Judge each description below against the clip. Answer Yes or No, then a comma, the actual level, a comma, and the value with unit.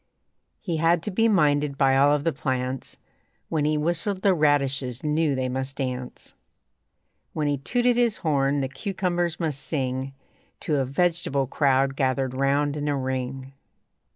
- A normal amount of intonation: Yes, average, 3.7 semitones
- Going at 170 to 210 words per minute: No, average, 155 wpm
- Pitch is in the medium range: Yes, medium, 145 Hz